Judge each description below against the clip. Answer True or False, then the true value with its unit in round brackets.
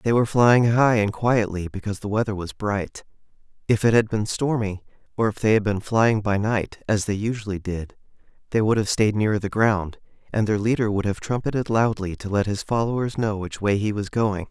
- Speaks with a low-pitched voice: True (105 Hz)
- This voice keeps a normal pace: False (215 wpm)